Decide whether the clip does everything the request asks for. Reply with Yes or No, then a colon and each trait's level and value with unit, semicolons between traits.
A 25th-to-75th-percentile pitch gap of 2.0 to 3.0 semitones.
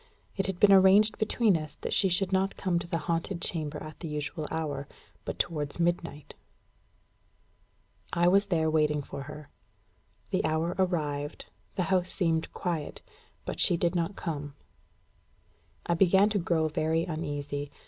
No: average, 3.4 semitones